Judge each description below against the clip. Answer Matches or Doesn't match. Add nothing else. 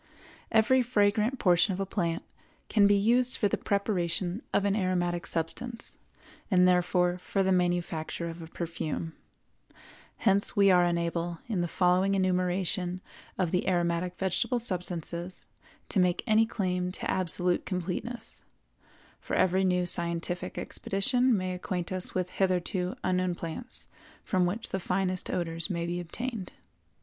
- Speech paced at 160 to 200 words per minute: Doesn't match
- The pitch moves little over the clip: Matches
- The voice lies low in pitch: Doesn't match